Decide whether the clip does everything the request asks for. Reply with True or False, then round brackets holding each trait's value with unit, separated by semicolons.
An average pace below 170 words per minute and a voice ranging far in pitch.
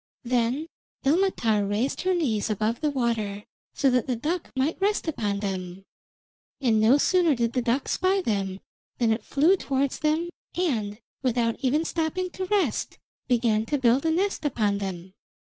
True (160 wpm; 6.7 semitones)